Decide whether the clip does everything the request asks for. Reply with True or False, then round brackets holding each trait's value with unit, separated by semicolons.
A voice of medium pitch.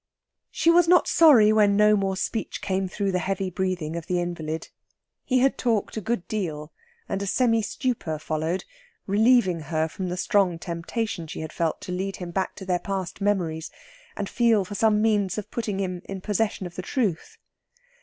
False (195 Hz)